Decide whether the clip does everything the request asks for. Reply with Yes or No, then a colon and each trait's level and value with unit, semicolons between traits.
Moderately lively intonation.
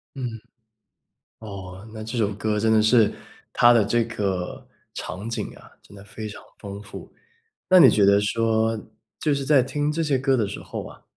Yes: average, 3.3 semitones